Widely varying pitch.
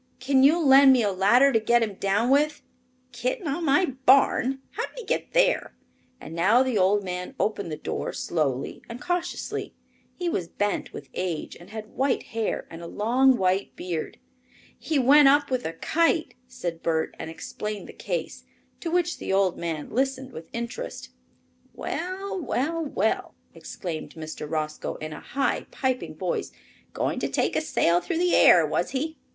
Yes: wide, 7.7 semitones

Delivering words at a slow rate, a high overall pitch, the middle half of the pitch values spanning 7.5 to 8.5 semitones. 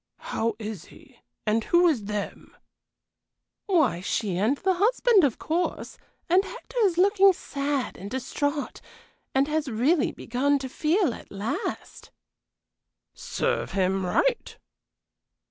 Yes: slow, 125 wpm; very high, 280 Hz; wide, 8.2 semitones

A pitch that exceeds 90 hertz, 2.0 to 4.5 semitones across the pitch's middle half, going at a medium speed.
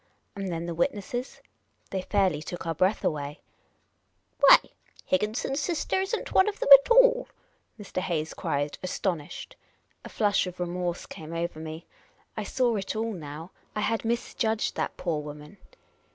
No: medium, 185 Hz; wide, 5.6 semitones; average, 160 wpm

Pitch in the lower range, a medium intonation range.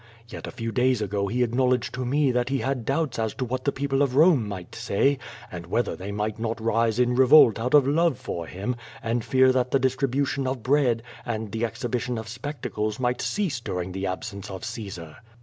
Yes: low, 120 Hz; average, 3.3 semitones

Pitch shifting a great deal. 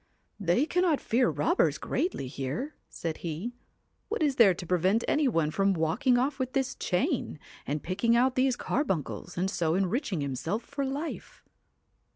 Yes: wide, 8.2 semitones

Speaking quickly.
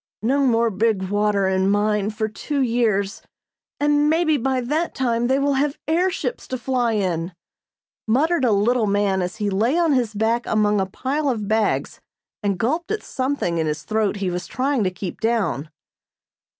No: average, 180 wpm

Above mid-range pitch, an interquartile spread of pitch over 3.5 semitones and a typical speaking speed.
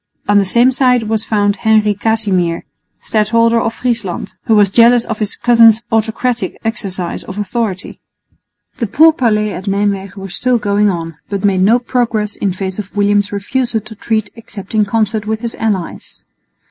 No: high, 215 Hz; narrow, 2.4 semitones; average, 165 wpm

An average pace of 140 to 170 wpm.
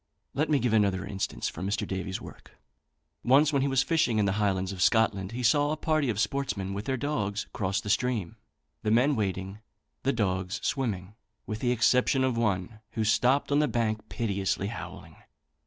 No: average, 190 wpm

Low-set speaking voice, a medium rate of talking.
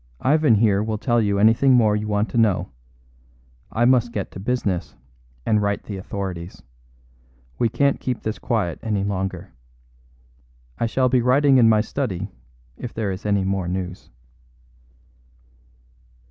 Yes: low, 105 Hz; average, 150 wpm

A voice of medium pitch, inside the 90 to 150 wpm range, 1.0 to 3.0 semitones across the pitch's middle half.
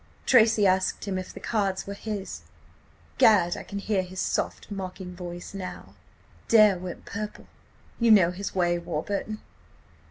No: high, 195 Hz; average, 140 wpm; narrow, 2.6 semitones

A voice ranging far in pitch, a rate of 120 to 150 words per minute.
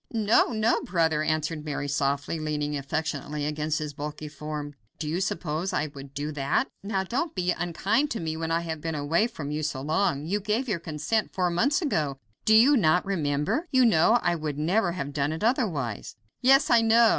No: wide, 5.8 semitones; average, 200 wpm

